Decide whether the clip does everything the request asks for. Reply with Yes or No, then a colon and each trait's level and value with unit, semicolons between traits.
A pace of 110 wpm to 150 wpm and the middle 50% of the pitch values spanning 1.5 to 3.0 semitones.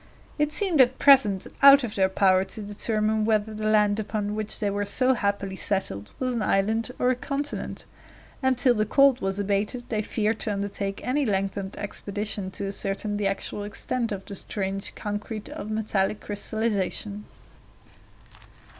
No: average, 165 wpm; narrow, 2.6 semitones